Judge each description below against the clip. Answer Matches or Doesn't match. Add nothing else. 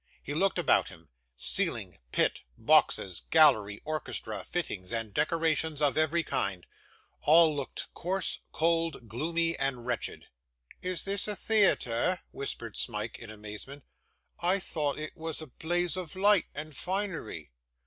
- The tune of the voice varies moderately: Doesn't match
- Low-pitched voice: Doesn't match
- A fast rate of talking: Doesn't match